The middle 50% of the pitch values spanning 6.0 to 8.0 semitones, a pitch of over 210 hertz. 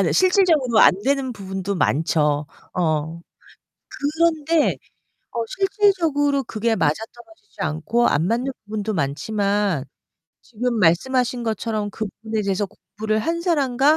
Yes: wide, 6.8 semitones; high, 225 Hz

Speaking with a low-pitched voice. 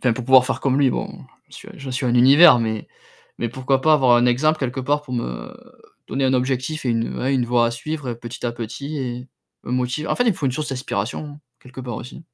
Yes: low, 130 Hz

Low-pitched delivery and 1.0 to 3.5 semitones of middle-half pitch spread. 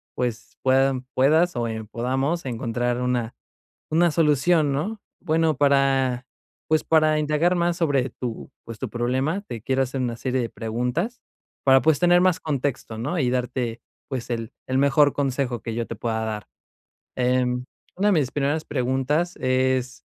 No: low, 130 Hz; average, 3.9 semitones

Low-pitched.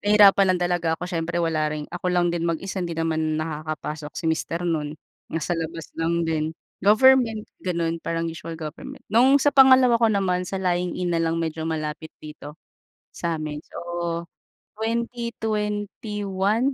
No: medium, 170 Hz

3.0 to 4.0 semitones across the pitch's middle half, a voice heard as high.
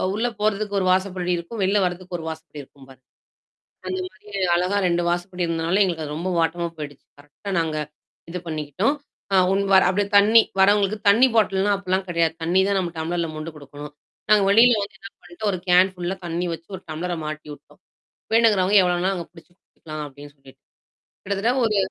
No: average, 3.6 semitones; medium, 180 Hz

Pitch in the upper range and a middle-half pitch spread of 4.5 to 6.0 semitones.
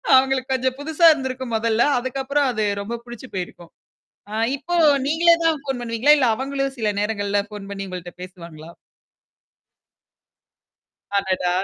Yes: high, 240 Hz; average, 5.1 semitones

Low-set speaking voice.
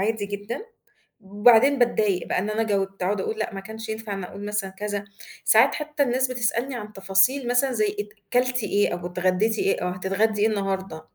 No: high, 210 Hz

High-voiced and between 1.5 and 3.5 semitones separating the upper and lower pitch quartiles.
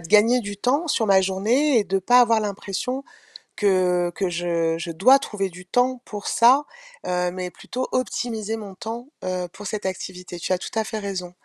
No: high, 200 Hz; average, 4.4 semitones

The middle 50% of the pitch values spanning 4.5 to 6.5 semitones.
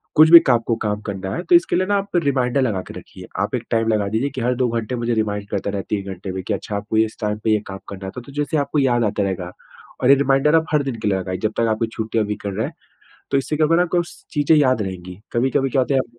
Yes: wide, 5.4 semitones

